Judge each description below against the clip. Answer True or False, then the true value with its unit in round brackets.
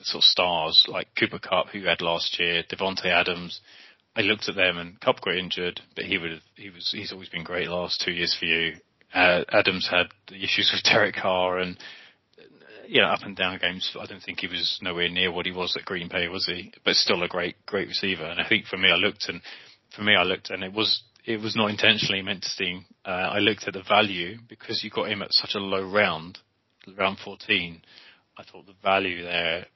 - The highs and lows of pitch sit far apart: False (2.5 semitones)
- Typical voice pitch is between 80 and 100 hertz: True (90 Hz)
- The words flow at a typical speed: False (230 wpm)